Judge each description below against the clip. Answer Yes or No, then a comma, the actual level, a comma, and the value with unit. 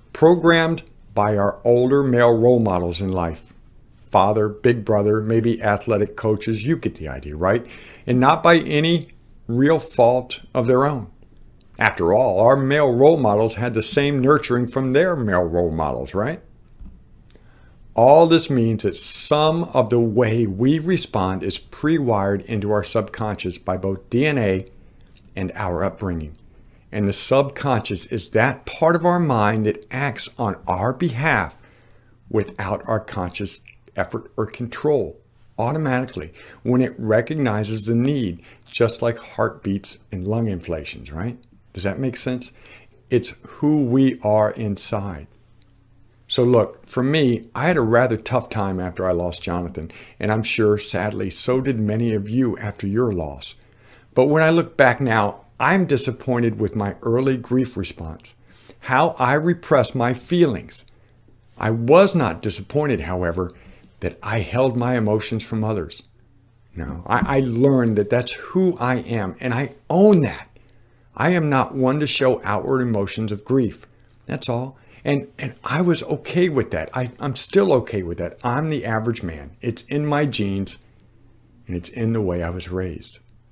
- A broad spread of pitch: No, average, 4.2 semitones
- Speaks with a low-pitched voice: Yes, low, 115 Hz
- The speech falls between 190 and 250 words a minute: No, average, 155 wpm